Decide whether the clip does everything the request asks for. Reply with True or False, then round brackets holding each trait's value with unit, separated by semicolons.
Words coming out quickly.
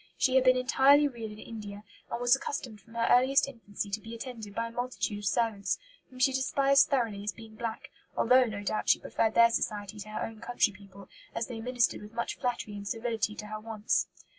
True (215 wpm)